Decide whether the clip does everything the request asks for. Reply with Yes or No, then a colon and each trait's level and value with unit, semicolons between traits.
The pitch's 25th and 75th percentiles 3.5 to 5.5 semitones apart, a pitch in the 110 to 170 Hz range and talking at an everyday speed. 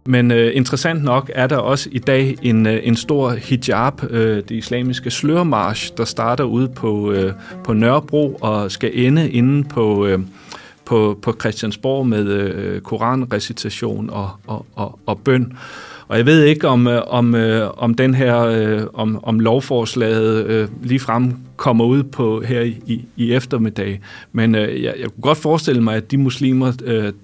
No: average, 3.0 semitones; low, 115 Hz; average, 165 wpm